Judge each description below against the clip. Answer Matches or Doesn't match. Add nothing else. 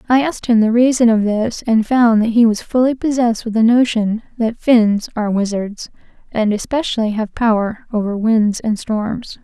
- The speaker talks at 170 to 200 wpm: Matches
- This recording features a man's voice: Doesn't match